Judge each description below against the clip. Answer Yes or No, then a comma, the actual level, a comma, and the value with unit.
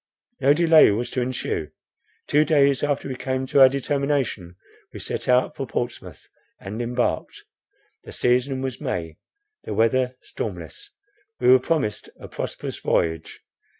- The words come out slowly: No, average, 145 wpm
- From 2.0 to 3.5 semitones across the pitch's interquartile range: Yes, average, 2.8 semitones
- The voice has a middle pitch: No, low, 130 Hz